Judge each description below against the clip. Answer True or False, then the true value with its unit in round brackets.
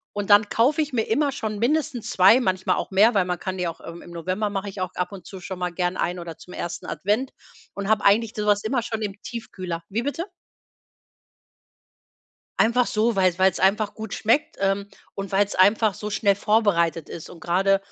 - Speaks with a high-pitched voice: True (200 Hz)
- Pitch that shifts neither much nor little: True (3.1 semitones)